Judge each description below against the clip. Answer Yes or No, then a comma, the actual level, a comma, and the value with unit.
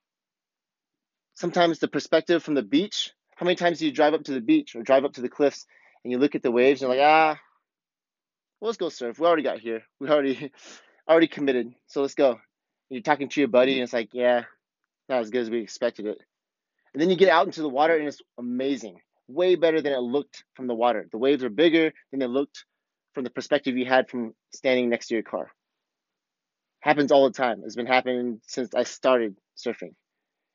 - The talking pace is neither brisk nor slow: No, fast, 220 wpm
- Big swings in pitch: No, average, 3.7 semitones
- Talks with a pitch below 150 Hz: Yes, low, 135 Hz